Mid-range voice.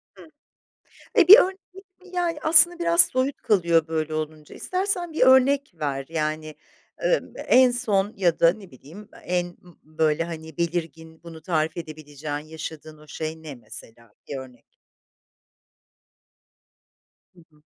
Yes: medium, 165 Hz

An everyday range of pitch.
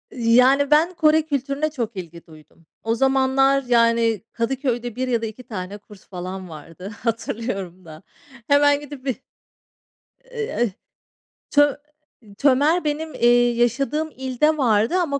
Yes: average, 4.5 semitones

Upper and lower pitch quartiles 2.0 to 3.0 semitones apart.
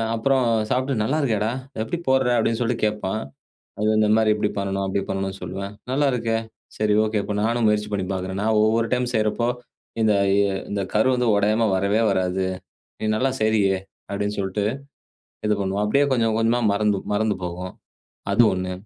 Yes: narrow, 2.4 semitones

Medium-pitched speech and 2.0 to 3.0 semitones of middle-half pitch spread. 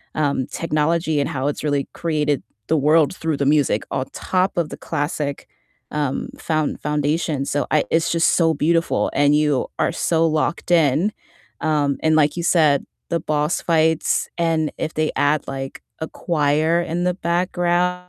Yes: medium, 155 Hz; narrow, 2.4 semitones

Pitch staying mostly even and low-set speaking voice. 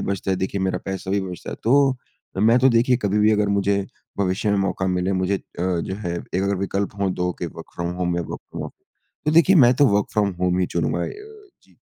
Yes: narrow, 2.1 semitones; very low, 95 Hz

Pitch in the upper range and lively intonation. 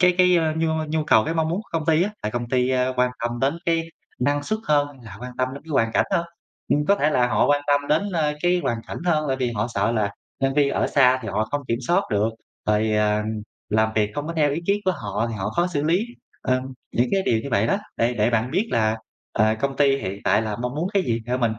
No: low, 130 Hz; wide, 5.9 semitones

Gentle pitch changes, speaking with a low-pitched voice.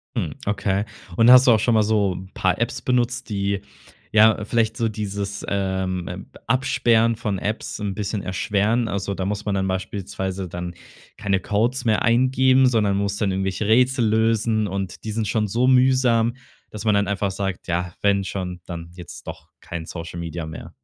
No: average, 3.0 semitones; low, 100 Hz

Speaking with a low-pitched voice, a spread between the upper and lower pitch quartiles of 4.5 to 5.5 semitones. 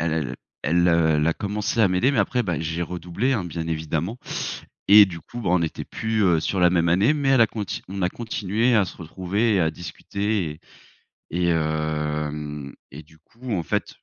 Yes: very low, 90 Hz; average, 4.9 semitones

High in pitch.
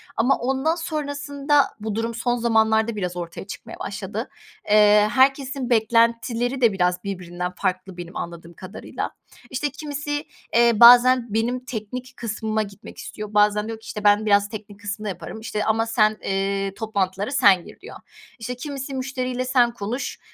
Yes: high, 220 Hz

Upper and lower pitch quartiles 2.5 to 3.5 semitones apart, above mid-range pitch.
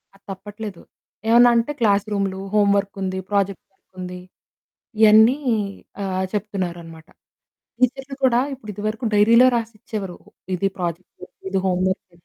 Yes: average, 2.8 semitones; high, 200 Hz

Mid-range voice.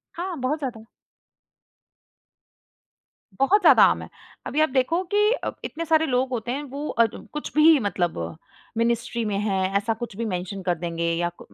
No: high, 240 Hz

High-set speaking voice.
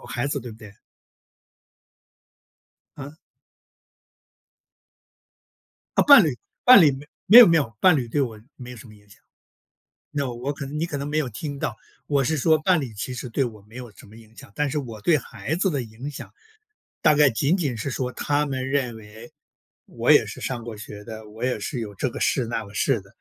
No: low, 130 Hz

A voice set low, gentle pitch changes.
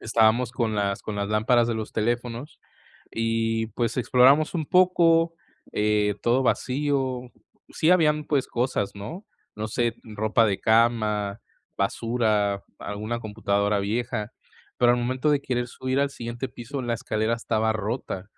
No: low, 115 Hz; average, 3.2 semitones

